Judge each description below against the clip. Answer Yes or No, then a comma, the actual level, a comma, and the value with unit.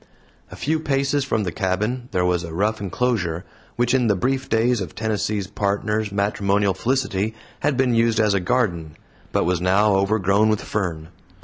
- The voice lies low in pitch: Yes, low, 105 Hz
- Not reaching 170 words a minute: No, average, 175 wpm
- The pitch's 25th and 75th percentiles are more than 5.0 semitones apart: No, average, 4.2 semitones